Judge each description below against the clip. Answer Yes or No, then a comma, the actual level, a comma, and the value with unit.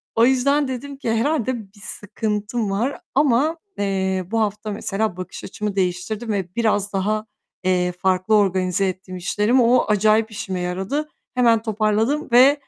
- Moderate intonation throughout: Yes, average, 3.9 semitones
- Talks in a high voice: Yes, high, 215 Hz